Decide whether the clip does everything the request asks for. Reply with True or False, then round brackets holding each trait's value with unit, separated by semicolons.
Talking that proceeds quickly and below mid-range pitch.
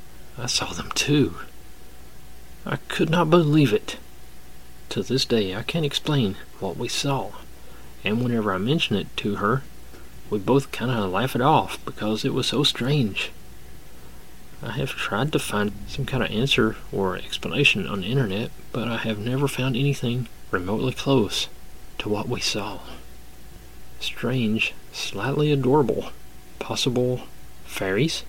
False (145 wpm; 115 Hz)